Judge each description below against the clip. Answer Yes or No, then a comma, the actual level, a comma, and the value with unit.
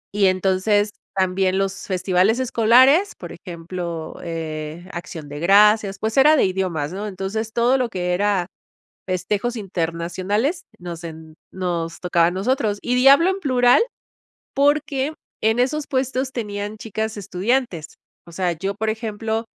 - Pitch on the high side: Yes, high, 200 Hz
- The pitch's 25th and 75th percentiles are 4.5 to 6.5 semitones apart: Yes, average, 5.0 semitones